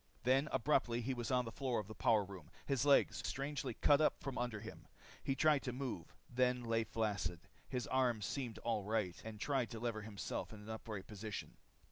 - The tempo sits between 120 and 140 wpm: No, fast, 205 wpm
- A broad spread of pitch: No, average, 3.3 semitones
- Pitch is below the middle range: Yes, low, 115 Hz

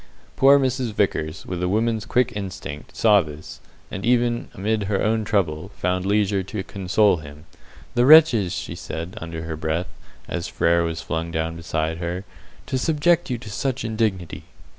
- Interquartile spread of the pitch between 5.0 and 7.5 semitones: Yes, wide, 5.4 semitones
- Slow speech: No, average, 165 wpm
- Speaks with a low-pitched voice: Yes, very low, 95 Hz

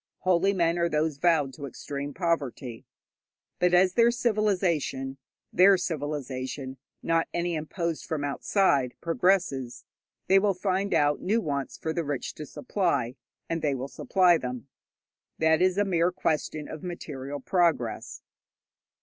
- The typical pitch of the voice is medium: Yes, medium, 165 Hz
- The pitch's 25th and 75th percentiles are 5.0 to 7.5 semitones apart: No, average, 4.5 semitones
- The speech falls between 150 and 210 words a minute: No, average, 140 wpm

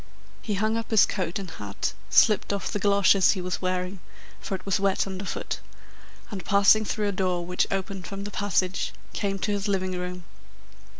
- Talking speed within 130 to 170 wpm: No, average, 185 wpm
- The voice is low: No, high, 195 Hz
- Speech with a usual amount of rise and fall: No, narrow, 1.6 semitones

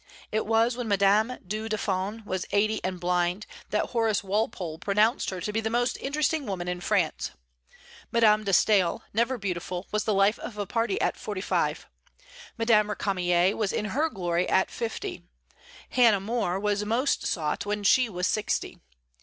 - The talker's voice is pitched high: Yes, high, 210 Hz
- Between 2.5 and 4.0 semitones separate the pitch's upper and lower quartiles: Yes, average, 3.1 semitones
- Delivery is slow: No, average, 170 wpm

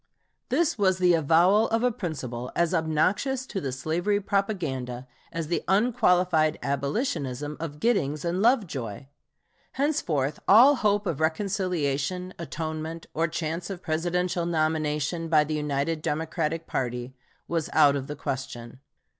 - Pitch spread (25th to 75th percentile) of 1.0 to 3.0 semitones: No, average, 4.2 semitones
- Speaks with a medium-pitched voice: Yes, medium, 165 Hz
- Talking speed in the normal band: No, slow, 130 wpm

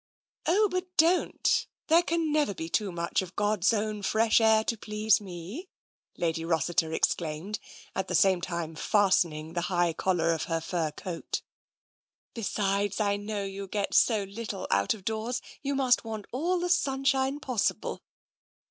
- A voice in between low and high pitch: No, high, 205 Hz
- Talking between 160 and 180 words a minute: Yes, average, 165 wpm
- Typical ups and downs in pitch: No, wide, 5.9 semitones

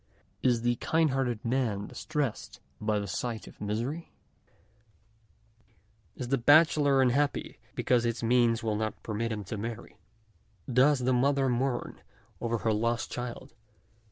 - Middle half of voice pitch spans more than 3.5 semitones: No, average, 2.9 semitones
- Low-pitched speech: Yes, low, 120 Hz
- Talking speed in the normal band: No, slow, 130 wpm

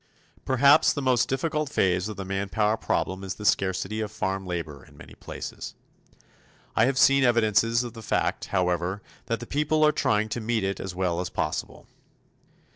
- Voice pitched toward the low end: Yes, low, 110 Hz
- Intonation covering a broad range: No, average, 4.5 semitones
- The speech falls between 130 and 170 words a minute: No, average, 180 wpm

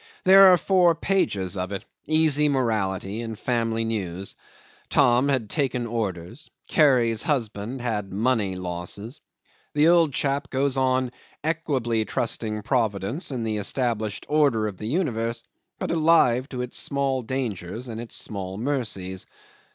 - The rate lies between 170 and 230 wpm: No, slow, 135 wpm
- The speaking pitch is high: No, low, 120 Hz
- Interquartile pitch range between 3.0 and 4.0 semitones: No, average, 4.8 semitones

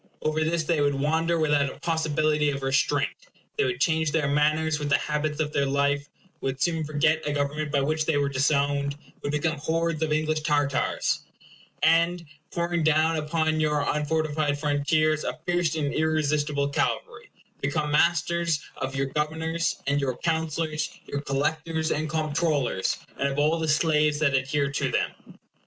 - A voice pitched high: No, medium, 155 Hz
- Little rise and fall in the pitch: Yes, narrow, 1.8 semitones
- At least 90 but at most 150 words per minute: No, average, 165 wpm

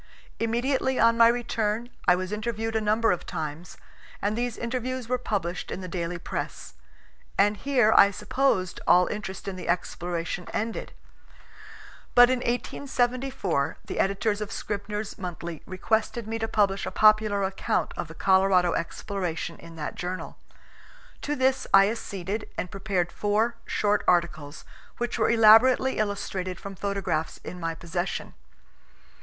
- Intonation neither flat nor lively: Yes, average, 4.1 semitones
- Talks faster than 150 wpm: No, average, 145 wpm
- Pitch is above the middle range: Yes, high, 205 Hz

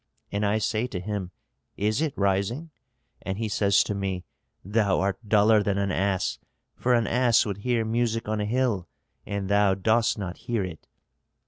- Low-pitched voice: Yes, low, 105 Hz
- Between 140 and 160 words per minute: No, average, 180 wpm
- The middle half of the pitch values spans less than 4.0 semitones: Yes, narrow, 2.6 semitones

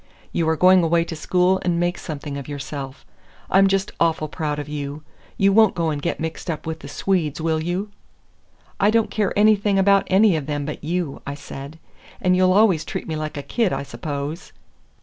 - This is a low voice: No, medium, 165 Hz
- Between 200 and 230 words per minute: Yes, fast, 205 wpm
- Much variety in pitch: No, average, 4.2 semitones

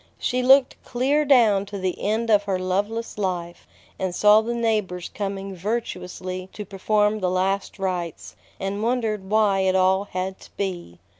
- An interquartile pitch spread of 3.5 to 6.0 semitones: No, average, 2.7 semitones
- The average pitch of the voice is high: Yes, high, 200 Hz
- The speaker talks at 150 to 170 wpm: Yes, average, 160 wpm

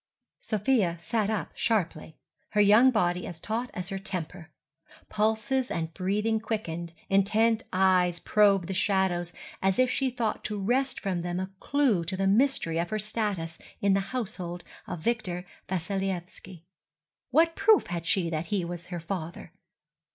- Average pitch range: Yes, average, 4.0 semitones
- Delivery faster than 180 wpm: No, average, 155 wpm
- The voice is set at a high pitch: Yes, high, 195 Hz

